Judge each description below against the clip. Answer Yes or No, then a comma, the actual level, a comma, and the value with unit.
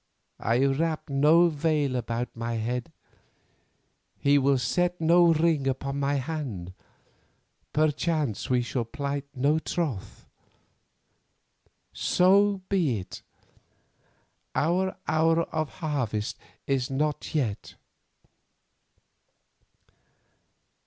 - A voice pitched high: No, medium, 145 Hz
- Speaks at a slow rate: Yes, slow, 90 wpm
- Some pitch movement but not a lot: Yes, average, 4.4 semitones